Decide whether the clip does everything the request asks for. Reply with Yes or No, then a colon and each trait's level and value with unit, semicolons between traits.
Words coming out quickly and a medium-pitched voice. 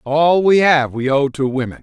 Yes: fast, 230 wpm; medium, 145 Hz